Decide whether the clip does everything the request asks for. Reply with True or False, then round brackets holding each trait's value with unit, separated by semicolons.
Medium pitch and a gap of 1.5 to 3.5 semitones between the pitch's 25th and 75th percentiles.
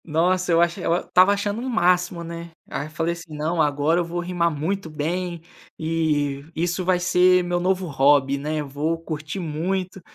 True (170 Hz; 2.8 semitones)